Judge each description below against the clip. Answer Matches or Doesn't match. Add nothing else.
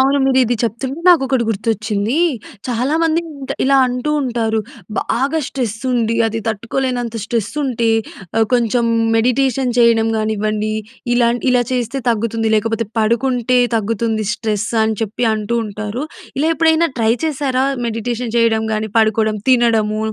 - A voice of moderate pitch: Doesn't match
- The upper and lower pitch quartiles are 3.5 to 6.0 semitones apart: Doesn't match